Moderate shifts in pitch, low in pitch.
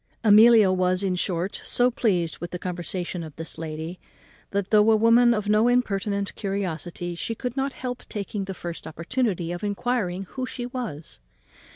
No: average, 4.6 semitones; high, 200 Hz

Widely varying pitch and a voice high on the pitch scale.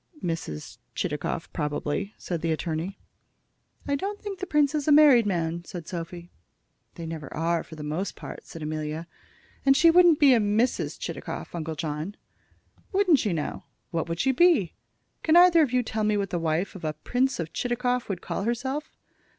Yes: wide, 8.7 semitones; high, 195 Hz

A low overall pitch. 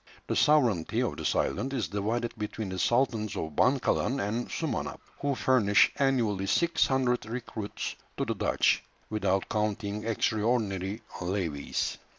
Yes: low, 110 Hz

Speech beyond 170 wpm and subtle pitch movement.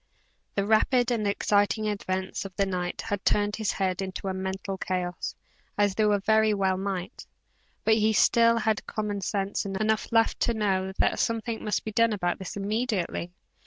No: average, 165 wpm; narrow, 2.3 semitones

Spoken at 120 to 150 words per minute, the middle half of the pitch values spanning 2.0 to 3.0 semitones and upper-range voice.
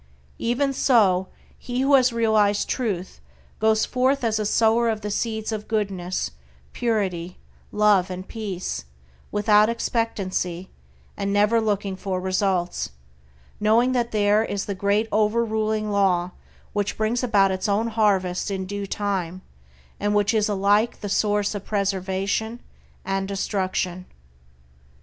Yes: slow, 135 wpm; narrow, 2.4 semitones; high, 205 Hz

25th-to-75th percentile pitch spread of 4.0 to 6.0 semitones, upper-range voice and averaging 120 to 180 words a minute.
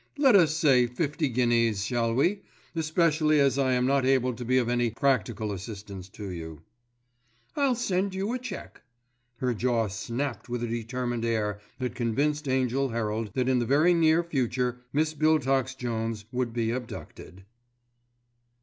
No: average, 4.4 semitones; low, 125 Hz; average, 160 wpm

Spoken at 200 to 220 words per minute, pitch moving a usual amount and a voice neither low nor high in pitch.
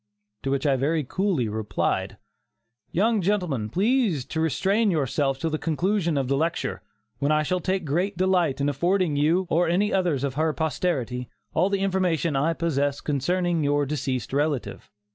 No: average, 165 wpm; average, 4.7 semitones; medium, 160 Hz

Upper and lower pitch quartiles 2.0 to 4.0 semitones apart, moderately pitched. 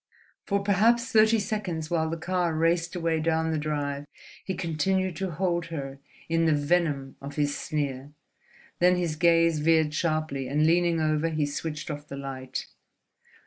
Yes: average, 2.8 semitones; medium, 160 Hz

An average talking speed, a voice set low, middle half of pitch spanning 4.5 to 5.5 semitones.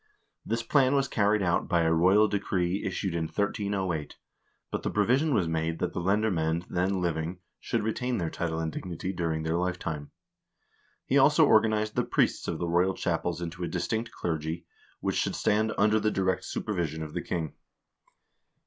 No: average, 175 wpm; very low, 90 Hz; average, 4.1 semitones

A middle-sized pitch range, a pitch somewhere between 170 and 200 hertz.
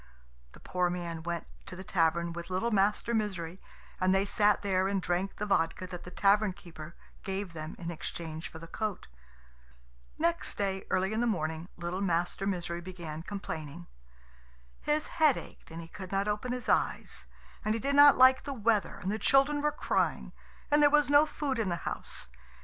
Yes: average, 4.4 semitones; high, 190 Hz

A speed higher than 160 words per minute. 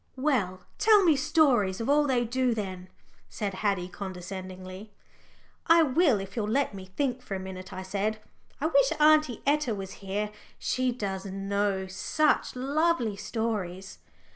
No: average, 150 wpm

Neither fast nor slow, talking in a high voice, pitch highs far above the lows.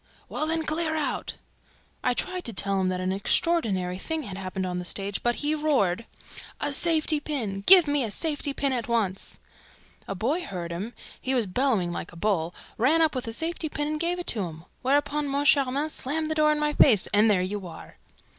No: fast, 210 wpm; very high, 255 Hz; wide, 7.7 semitones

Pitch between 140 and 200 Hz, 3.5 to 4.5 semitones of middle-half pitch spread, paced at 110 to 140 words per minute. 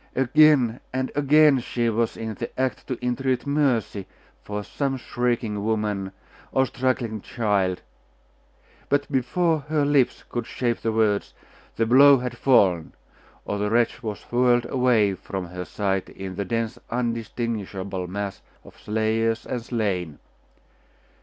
No: low, 115 Hz; average, 3.8 semitones; slow, 135 wpm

